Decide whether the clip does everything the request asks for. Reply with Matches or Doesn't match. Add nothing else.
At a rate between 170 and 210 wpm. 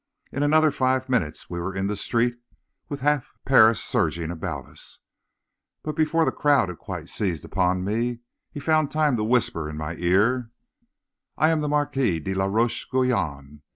Matches